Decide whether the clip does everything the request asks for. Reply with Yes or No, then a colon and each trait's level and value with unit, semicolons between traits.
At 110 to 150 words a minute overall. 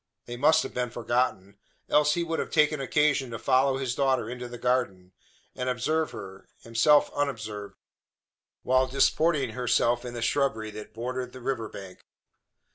No: average, 160 wpm